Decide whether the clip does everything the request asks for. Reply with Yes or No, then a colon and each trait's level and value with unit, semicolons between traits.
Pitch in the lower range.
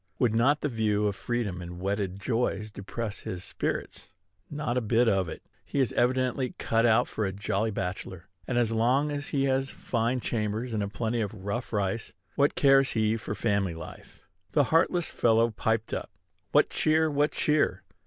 Yes: low, 115 Hz